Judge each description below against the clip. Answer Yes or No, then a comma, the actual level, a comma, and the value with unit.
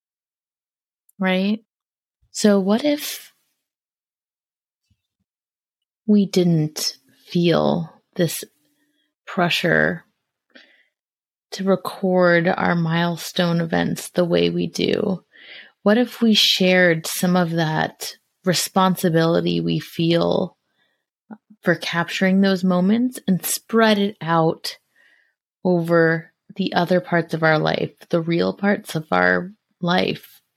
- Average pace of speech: No, slow, 95 wpm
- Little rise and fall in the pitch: No, average, 3.5 semitones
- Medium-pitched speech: Yes, medium, 180 Hz